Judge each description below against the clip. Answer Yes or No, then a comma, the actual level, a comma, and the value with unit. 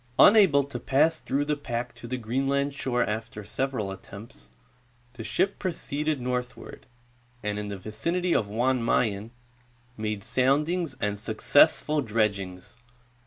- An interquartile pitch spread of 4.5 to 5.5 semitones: Yes, average, 5.1 semitones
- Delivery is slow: Yes, slow, 130 wpm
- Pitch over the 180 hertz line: No, low, 125 Hz